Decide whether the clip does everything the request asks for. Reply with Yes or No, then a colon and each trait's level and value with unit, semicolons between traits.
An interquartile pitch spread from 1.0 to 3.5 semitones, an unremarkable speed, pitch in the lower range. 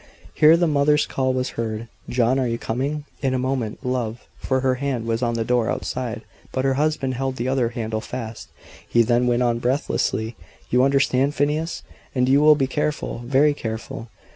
Yes: average, 2.7 semitones; average, 190 wpm; low, 130 Hz